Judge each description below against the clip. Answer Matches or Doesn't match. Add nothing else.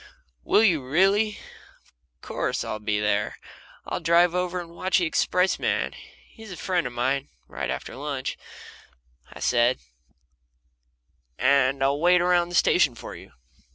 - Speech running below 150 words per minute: Matches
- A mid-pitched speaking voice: Matches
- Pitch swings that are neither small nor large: Doesn't match